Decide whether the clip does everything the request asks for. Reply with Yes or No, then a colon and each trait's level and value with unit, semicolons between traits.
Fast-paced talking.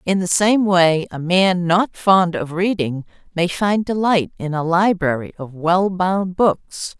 No: average, 170 wpm